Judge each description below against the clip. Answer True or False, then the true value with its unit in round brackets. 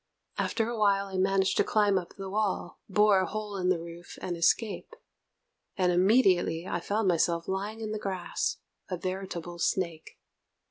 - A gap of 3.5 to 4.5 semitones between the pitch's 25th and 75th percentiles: False (2.9 semitones)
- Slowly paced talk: False (170 wpm)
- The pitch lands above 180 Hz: True (190 Hz)